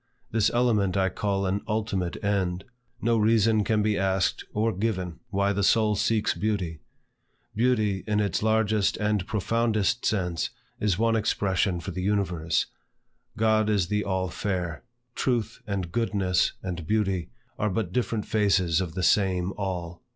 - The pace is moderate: Yes, average, 150 wpm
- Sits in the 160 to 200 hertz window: No, low, 100 Hz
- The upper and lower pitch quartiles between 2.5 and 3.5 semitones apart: Yes, average, 2.8 semitones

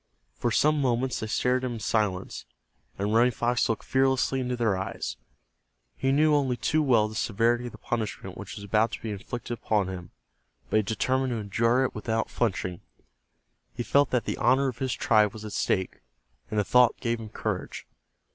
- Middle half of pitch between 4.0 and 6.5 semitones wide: No, average, 3.1 semitones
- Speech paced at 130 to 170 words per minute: No, average, 195 wpm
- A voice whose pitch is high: No, low, 115 Hz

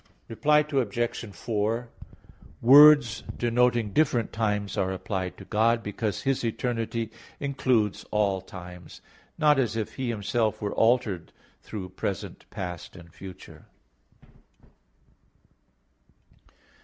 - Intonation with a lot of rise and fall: No, average, 3.4 semitones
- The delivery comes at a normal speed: No, slow, 105 wpm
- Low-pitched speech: Yes, low, 115 Hz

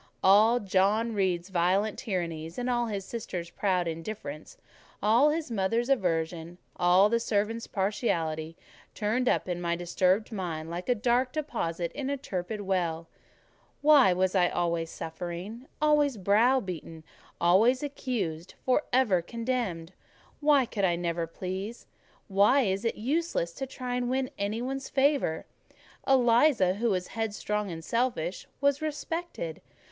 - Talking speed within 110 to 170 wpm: Yes, slow, 135 wpm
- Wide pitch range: Yes, wide, 5.9 semitones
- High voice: Yes, high, 205 Hz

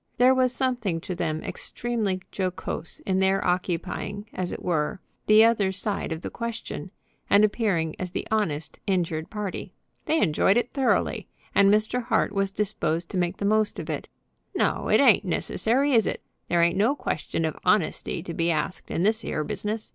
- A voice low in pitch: No, high, 195 Hz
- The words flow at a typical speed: Yes, average, 180 wpm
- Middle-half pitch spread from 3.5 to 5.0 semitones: Yes, average, 4.4 semitones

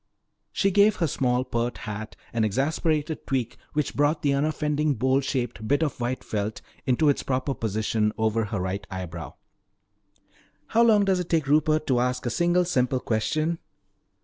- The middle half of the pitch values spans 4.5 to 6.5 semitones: Yes, wide, 5.4 semitones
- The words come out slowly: No, average, 165 wpm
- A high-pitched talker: No, low, 135 Hz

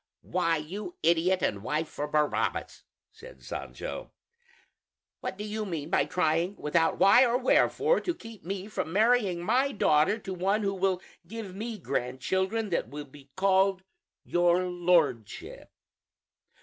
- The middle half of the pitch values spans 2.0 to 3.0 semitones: No, average, 4.4 semitones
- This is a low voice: No, medium, 185 Hz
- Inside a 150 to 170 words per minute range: No, average, 140 wpm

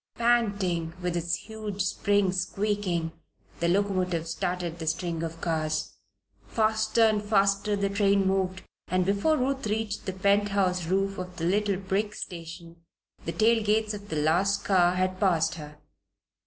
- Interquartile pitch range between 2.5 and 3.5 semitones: Yes, average, 2.9 semitones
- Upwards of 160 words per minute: No, average, 155 wpm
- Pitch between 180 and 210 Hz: Yes, high, 190 Hz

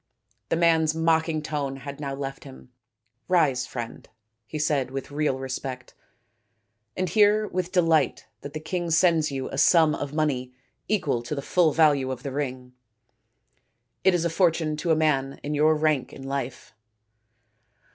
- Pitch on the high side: No, medium, 150 Hz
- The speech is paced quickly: No, average, 170 wpm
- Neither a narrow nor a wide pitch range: Yes, average, 3.3 semitones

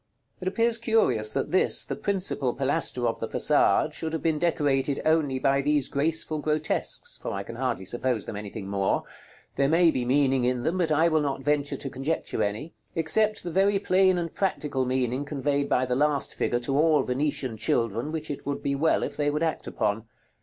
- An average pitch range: Yes, average, 4.0 semitones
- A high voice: No, medium, 145 Hz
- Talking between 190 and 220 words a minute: Yes, average, 200 wpm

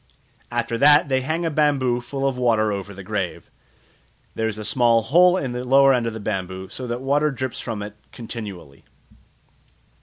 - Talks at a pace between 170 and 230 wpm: Yes, average, 190 wpm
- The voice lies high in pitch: No, low, 120 Hz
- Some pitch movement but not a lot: Yes, average, 4.2 semitones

